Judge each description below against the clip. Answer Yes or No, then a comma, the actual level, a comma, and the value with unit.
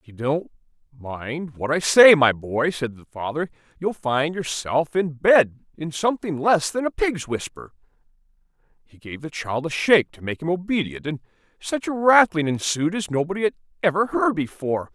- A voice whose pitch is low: No, medium, 160 Hz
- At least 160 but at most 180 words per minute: Yes, average, 175 wpm